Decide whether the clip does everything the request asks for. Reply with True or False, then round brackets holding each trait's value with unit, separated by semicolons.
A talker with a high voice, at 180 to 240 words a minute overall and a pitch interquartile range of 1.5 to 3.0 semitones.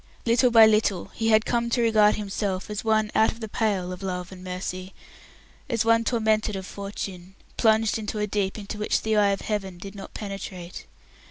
True (210 Hz; 195 wpm; 2.4 semitones)